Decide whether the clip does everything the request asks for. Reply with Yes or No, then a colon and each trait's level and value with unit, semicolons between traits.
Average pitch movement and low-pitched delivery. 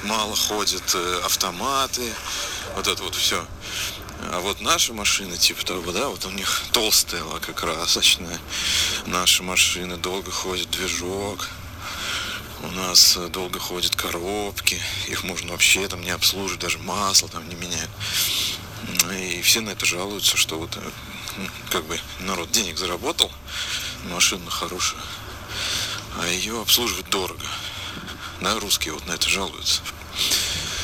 No: narrow, 2.3 semitones; very low, 95 Hz